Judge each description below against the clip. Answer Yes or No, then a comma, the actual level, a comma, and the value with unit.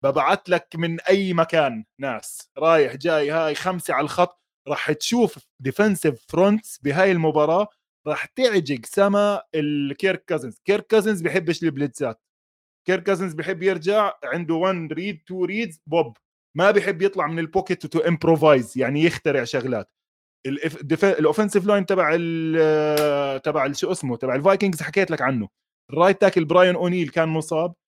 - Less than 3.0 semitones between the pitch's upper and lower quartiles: No, average, 4.0 semitones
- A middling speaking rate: No, fast, 140 wpm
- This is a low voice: No, medium, 170 Hz